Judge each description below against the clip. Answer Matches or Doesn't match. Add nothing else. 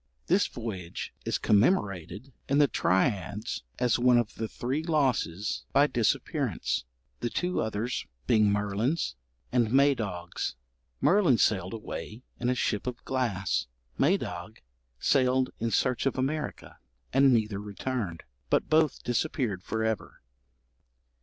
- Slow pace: Matches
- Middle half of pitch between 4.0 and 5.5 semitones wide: Matches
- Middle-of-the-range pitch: Doesn't match